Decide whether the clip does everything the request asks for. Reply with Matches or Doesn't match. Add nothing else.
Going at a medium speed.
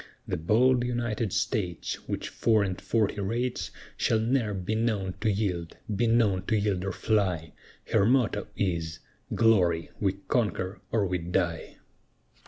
Matches